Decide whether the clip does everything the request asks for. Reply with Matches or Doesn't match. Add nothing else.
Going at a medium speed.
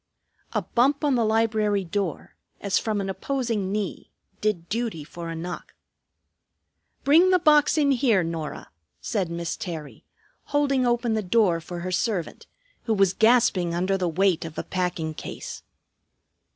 Matches